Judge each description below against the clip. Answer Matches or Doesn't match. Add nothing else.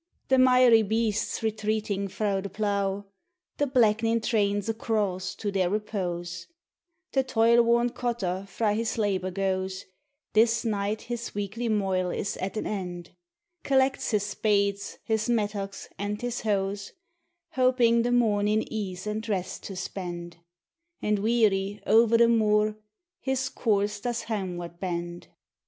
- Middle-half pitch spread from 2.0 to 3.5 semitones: Matches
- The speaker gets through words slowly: Doesn't match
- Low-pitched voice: Doesn't match